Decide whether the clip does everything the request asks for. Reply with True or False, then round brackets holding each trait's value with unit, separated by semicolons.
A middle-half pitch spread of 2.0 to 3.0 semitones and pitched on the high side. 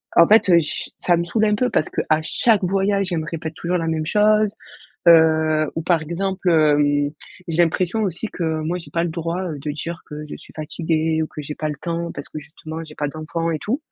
False (2.5 semitones; 165 Hz)